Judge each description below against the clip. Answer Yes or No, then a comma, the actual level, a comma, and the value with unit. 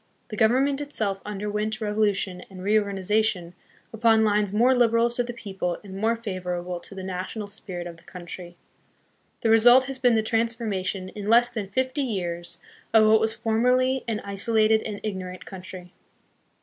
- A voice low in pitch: No, high, 215 Hz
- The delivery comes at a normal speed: Yes, average, 160 wpm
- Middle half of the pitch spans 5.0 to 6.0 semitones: No, average, 3.3 semitones